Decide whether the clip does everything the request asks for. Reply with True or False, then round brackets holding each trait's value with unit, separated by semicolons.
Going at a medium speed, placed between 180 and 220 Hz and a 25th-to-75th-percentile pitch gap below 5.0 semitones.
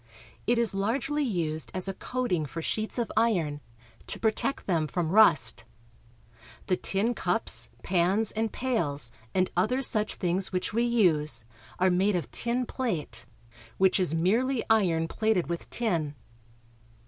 False (145 wpm; 190 Hz; 5.3 semitones)